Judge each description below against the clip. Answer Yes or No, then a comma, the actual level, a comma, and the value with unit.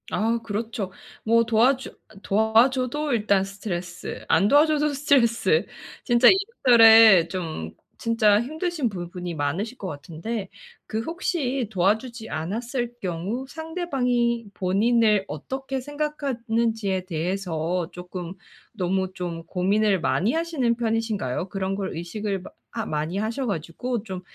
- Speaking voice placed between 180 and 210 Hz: No, high, 220 Hz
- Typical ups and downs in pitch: Yes, average, 5.0 semitones